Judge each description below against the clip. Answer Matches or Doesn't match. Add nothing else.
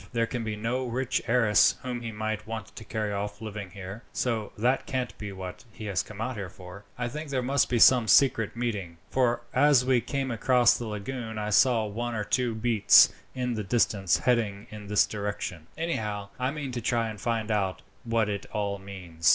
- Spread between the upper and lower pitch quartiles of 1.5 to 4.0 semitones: Matches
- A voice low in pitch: Matches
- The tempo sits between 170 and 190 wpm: Doesn't match